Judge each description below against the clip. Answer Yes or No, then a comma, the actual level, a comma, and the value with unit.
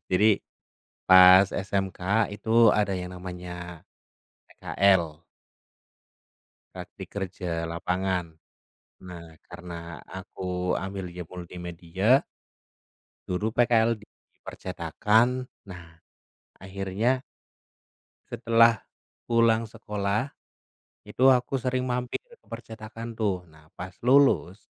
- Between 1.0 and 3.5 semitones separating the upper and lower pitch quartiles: No, average, 4.2 semitones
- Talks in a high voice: No, very low, 95 Hz